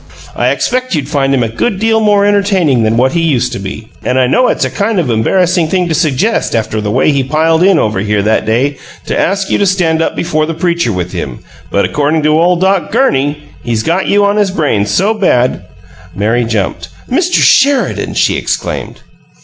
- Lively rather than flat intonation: Yes, wide, 8.7 semitones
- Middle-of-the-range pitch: Yes, medium, 155 Hz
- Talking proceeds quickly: Yes, fast, 215 wpm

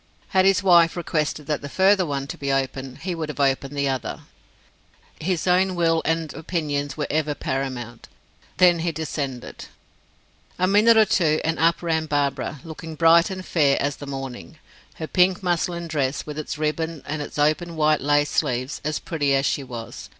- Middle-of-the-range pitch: Yes, medium, 155 Hz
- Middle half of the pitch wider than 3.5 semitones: No, average, 3.2 semitones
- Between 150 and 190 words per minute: Yes, average, 180 wpm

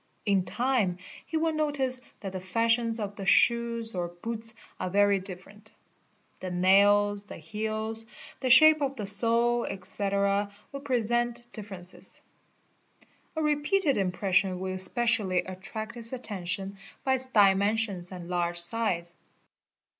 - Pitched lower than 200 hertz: No, high, 210 Hz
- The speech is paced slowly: Yes, slow, 130 wpm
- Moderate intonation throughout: Yes, average, 4.0 semitones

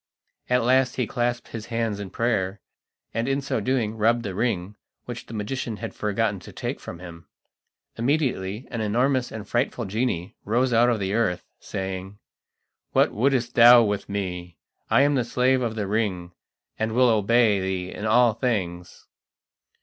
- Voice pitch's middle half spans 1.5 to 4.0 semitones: Yes, average, 3.6 semitones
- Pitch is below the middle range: Yes, low, 110 Hz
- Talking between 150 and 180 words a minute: Yes, average, 165 wpm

